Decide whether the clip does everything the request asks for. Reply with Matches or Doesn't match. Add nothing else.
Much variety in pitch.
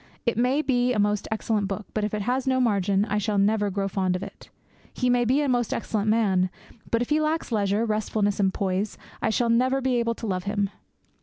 Doesn't match